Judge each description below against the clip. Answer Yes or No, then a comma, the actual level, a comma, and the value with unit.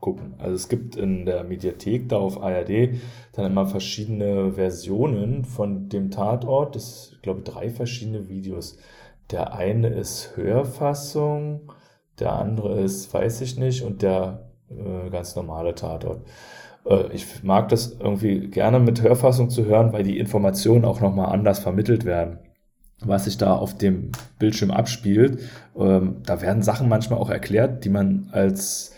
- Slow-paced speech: No, average, 155 wpm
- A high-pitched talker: No, low, 105 Hz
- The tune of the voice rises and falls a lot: No, average, 3.6 semitones